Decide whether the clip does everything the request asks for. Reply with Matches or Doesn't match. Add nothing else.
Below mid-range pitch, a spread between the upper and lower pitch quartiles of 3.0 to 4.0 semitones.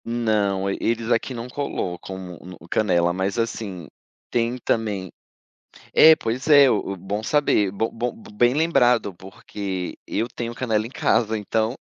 Matches